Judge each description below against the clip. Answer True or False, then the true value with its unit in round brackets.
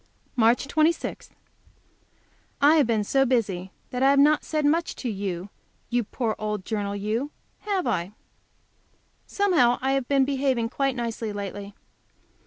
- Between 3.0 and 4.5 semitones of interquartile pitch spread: False (5.0 semitones)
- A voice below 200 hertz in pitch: False (245 Hz)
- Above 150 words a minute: False (145 wpm)